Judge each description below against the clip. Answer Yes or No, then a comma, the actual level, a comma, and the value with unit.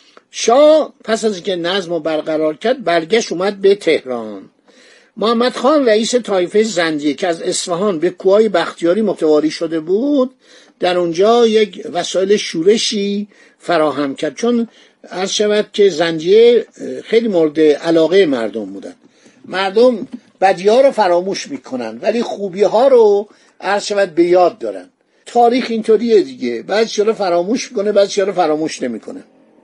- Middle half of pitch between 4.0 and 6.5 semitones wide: Yes, average, 5.2 semitones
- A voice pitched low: No, high, 200 Hz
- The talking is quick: No, average, 140 wpm